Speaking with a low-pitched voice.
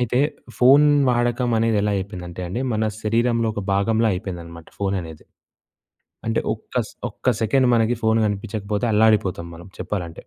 Yes: low, 110 Hz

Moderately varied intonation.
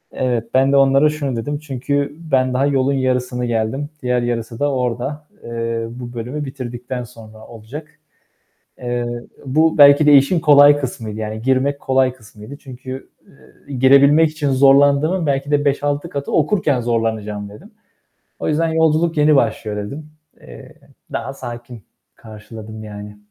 Yes: average, 3.6 semitones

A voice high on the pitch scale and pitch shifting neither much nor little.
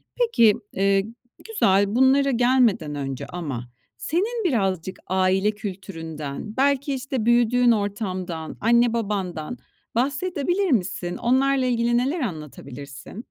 No: high, 220 Hz; wide, 6.0 semitones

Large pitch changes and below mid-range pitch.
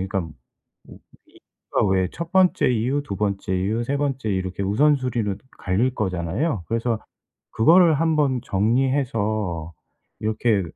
Yes: wide, 5.8 semitones; low, 110 Hz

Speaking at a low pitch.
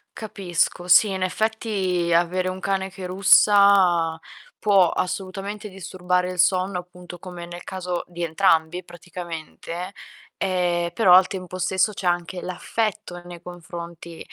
No: medium, 180 Hz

